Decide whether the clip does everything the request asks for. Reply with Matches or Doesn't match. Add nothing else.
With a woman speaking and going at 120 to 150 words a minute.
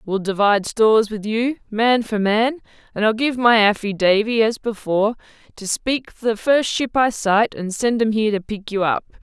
Doesn't match